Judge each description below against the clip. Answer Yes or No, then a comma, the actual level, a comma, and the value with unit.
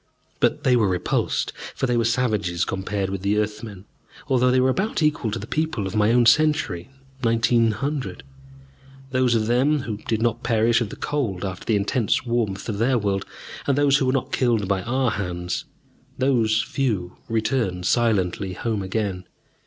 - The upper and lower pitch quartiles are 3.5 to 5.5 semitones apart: Yes, average, 4.2 semitones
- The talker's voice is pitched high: No, low, 115 Hz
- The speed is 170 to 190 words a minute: Yes, average, 175 wpm